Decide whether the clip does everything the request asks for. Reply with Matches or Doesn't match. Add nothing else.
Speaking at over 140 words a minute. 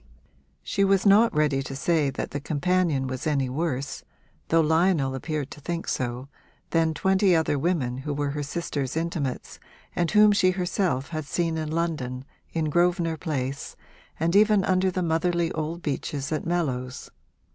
Matches